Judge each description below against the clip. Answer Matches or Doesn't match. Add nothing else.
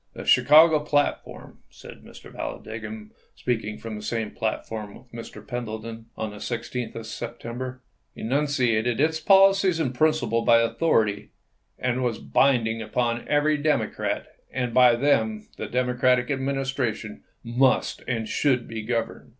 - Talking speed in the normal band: Matches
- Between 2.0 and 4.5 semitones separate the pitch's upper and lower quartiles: Matches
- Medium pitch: Doesn't match